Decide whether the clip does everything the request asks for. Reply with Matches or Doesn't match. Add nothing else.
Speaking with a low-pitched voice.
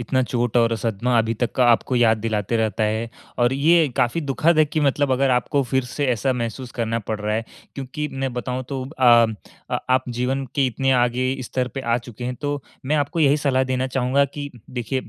Matches